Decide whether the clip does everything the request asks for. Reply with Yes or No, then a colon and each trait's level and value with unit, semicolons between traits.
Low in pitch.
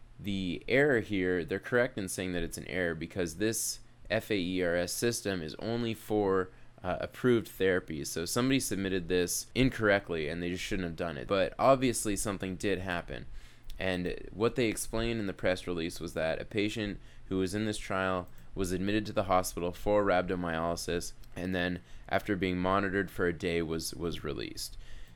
Yes: very low, 95 Hz